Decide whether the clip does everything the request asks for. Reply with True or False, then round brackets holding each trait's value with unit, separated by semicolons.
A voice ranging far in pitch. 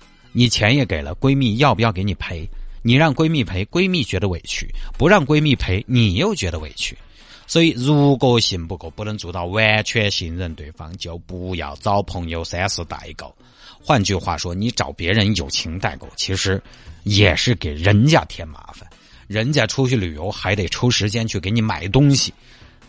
True (5.8 semitones)